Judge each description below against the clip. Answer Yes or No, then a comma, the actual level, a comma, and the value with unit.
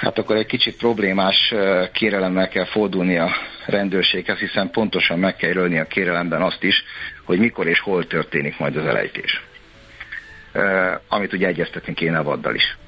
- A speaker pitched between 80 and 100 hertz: Yes, very low, 95 Hz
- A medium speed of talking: No, fast, 160 wpm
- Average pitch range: Yes, average, 3.0 semitones